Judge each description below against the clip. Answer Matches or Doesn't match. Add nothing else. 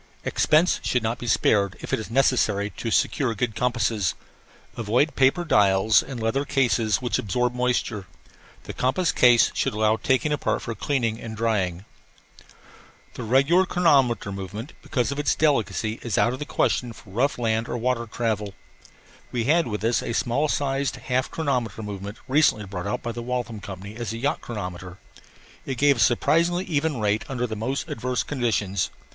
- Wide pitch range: Doesn't match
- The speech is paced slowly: Doesn't match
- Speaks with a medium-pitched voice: Doesn't match